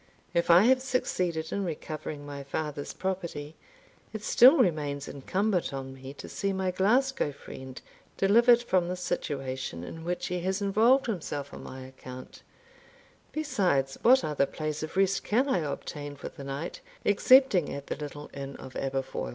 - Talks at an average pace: Yes, average, 160 wpm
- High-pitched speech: No, medium, 165 Hz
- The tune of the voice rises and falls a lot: Yes, wide, 5.9 semitones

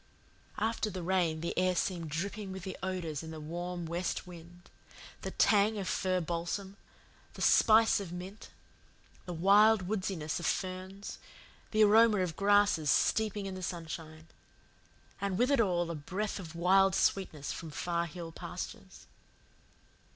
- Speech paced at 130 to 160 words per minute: Yes, average, 145 wpm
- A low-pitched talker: No, medium, 185 Hz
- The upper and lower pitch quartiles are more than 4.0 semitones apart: No, average, 3.0 semitones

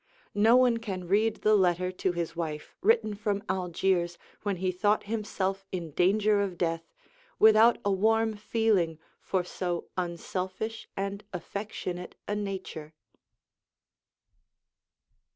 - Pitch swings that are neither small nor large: Yes, average, 3.2 semitones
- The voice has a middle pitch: No, high, 195 Hz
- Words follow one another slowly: Yes, slow, 120 wpm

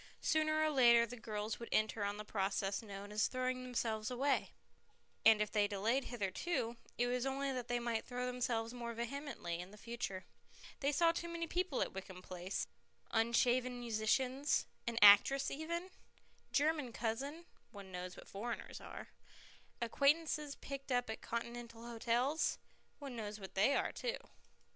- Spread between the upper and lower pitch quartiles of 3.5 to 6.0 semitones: Yes, average, 4.3 semitones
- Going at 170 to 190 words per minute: No, average, 160 wpm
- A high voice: Yes, high, 235 Hz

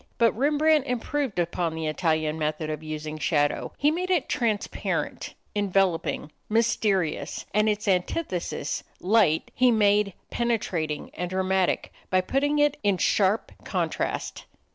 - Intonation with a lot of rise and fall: Yes, wide, 6.4 semitones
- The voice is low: No, high, 195 Hz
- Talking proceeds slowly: Yes, slow, 125 wpm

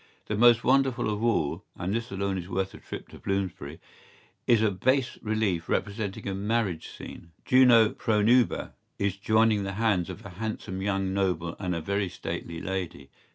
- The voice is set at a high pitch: No, low, 100 Hz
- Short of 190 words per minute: Yes, average, 175 wpm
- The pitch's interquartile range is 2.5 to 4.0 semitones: Yes, average, 3.2 semitones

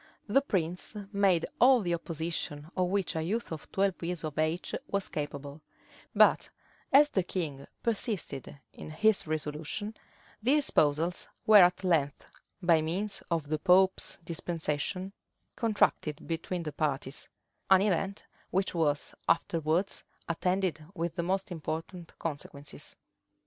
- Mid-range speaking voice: Yes, medium, 170 Hz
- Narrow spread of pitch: No, average, 3.7 semitones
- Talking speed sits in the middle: No, slow, 130 wpm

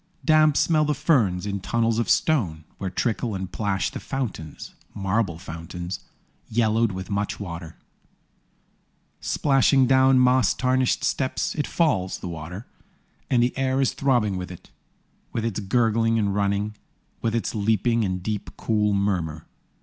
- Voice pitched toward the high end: No, low, 110 Hz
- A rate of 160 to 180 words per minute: No, average, 145 wpm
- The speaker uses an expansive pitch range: No, average, 5.0 semitones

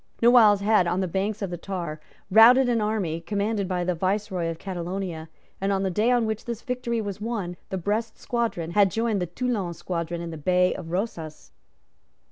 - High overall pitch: Yes, high, 195 Hz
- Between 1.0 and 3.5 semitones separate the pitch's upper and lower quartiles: No, average, 4.0 semitones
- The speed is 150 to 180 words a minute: No, average, 195 wpm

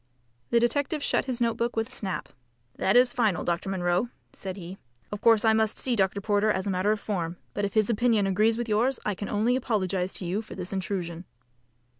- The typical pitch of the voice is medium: No, high, 210 Hz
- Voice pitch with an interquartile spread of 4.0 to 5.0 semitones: No, average, 3.5 semitones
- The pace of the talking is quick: Yes, fast, 220 wpm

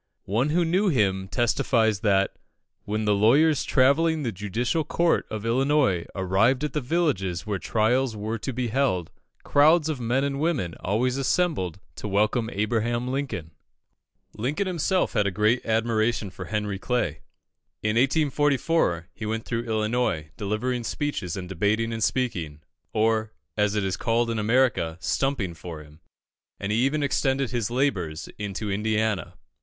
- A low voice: Yes, low, 115 Hz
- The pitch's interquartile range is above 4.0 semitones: Yes, average, 4.9 semitones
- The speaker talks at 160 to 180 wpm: No, average, 150 wpm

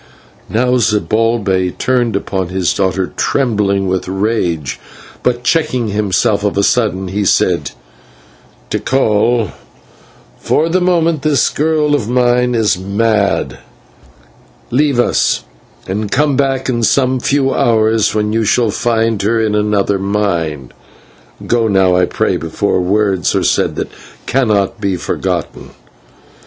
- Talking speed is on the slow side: Yes, slow, 125 wpm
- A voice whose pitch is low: Yes, low, 110 Hz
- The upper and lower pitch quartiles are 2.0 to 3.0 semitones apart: No, average, 4.1 semitones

